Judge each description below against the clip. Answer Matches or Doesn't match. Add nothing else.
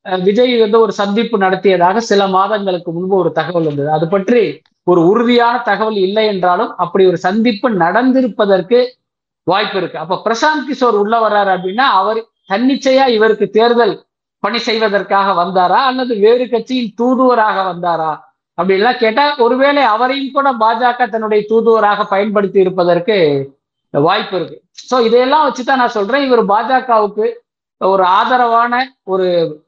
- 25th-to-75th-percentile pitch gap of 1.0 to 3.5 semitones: Doesn't match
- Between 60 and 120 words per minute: Doesn't match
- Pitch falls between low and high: Doesn't match